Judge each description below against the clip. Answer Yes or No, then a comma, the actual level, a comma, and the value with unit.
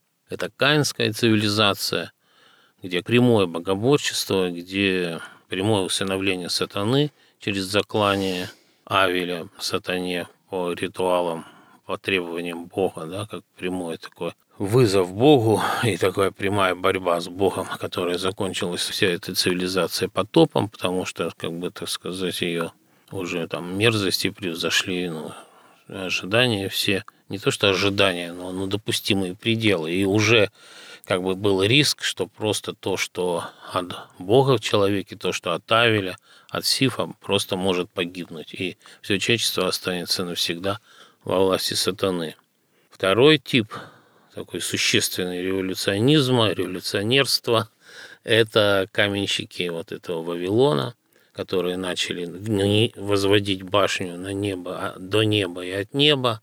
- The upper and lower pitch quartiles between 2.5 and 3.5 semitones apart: Yes, average, 2.9 semitones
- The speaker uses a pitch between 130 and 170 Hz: No, very low, 95 Hz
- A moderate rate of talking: Yes, average, 120 wpm